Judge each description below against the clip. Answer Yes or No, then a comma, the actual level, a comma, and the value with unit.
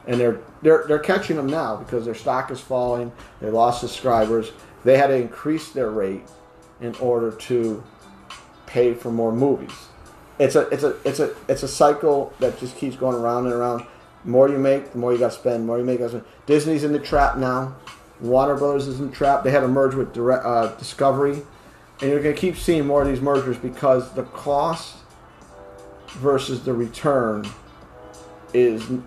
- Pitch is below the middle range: Yes, low, 130 Hz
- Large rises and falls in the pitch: No, average, 3.0 semitones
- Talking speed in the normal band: Yes, average, 195 wpm